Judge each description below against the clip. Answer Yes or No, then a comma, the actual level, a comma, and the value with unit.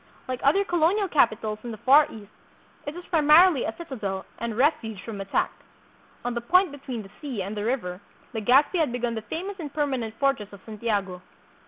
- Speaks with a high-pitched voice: Yes, high, 245 Hz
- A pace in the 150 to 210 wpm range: Yes, average, 185 wpm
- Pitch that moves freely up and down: Yes, wide, 5.9 semitones